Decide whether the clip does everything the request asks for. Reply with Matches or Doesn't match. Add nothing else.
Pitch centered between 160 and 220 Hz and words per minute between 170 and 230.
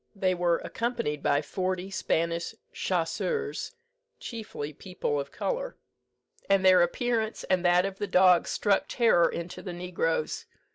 Doesn't match